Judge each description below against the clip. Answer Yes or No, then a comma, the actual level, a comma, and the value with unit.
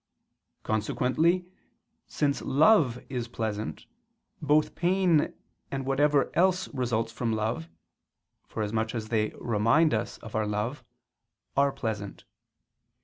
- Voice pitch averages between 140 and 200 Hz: No, low, 120 Hz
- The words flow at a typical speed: No, slow, 105 wpm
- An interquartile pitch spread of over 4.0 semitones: Yes, average, 5.2 semitones